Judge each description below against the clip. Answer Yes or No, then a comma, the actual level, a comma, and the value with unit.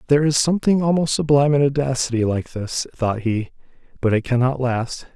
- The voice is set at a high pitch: No, low, 130 Hz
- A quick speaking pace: No, average, 175 wpm